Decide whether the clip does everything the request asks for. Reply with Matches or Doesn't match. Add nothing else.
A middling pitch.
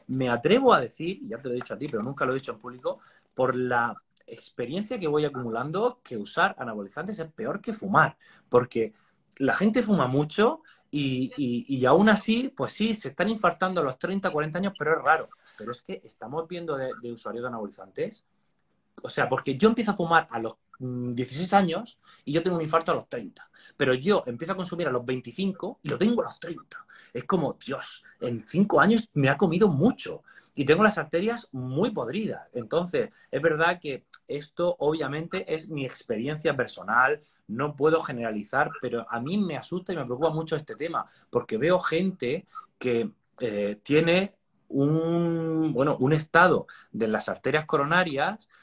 Matches